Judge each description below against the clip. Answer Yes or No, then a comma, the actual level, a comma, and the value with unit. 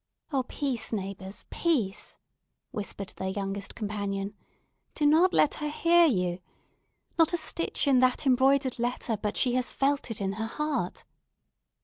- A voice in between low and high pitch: No, high, 245 Hz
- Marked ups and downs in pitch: Yes, wide, 6.3 semitones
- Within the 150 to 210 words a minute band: No, average, 140 wpm